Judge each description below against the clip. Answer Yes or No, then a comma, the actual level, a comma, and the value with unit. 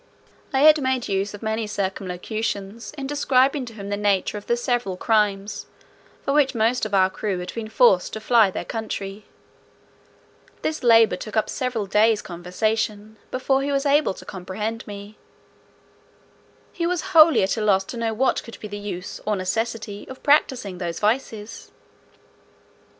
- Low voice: No, high, 220 Hz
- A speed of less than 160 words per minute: No, average, 165 wpm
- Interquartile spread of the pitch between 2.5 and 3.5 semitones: No, average, 3.9 semitones